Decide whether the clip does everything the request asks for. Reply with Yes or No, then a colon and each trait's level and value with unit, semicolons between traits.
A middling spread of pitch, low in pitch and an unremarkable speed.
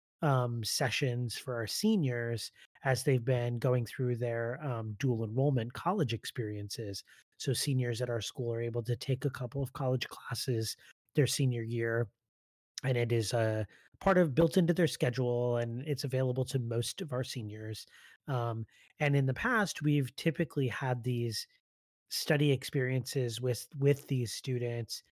Yes: average, 3.0 semitones; low, 125 Hz; average, 155 wpm